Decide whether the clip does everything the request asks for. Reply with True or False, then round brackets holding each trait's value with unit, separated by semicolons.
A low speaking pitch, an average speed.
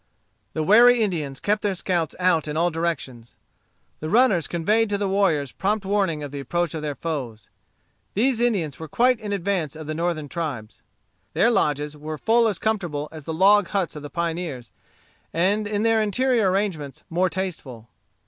False (175 Hz; 175 wpm)